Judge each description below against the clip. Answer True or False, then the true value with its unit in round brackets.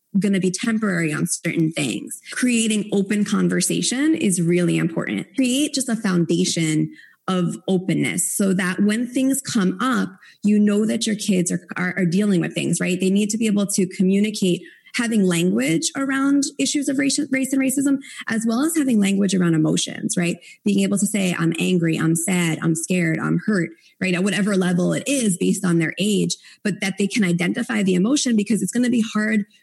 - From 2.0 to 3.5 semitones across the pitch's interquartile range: False (4.0 semitones)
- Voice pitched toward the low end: False (200 Hz)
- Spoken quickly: False (195 wpm)